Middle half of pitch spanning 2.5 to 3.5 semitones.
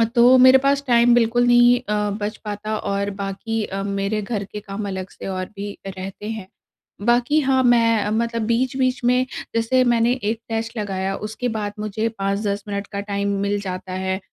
Yes: average, 3.2 semitones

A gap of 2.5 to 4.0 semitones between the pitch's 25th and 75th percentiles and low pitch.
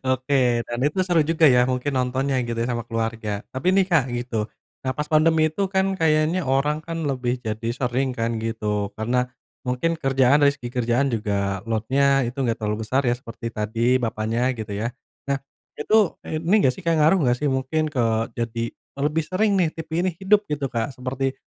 No: average, 4.6 semitones; low, 130 Hz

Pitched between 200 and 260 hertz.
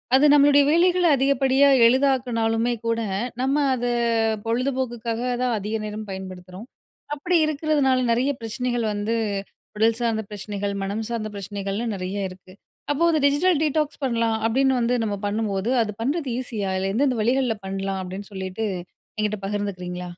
Yes: high, 230 Hz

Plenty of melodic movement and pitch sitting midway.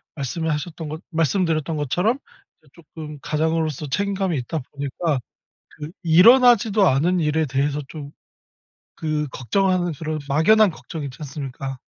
No: average, 3.5 semitones; medium, 155 Hz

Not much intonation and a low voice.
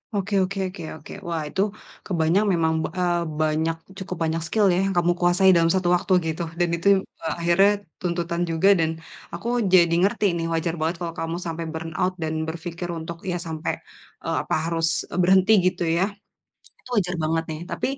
No: narrow, 2.0 semitones; medium, 170 Hz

